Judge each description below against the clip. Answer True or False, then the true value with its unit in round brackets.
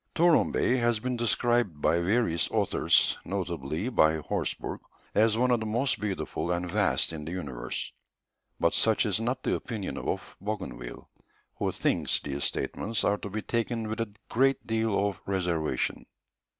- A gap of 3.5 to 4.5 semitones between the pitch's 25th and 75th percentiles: False (5.3 semitones)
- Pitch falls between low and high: False (105 Hz)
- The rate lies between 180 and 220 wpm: False (160 wpm)